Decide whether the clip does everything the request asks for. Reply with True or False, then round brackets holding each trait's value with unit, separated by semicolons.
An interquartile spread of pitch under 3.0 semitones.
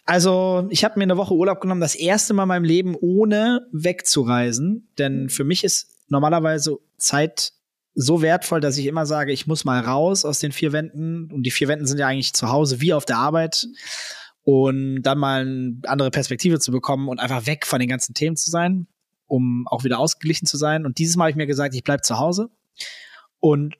False (4.6 semitones)